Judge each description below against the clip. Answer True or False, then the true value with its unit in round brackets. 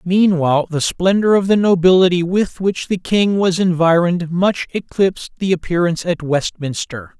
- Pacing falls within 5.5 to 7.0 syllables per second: False (5.0 syllables/s)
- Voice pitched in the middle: True (180 Hz)